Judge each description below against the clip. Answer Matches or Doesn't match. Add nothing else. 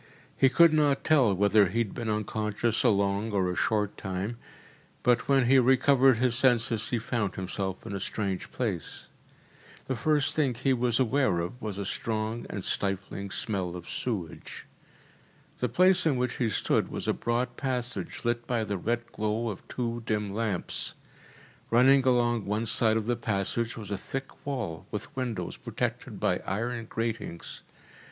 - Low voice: Matches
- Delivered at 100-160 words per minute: Doesn't match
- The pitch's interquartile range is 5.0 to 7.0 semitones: Doesn't match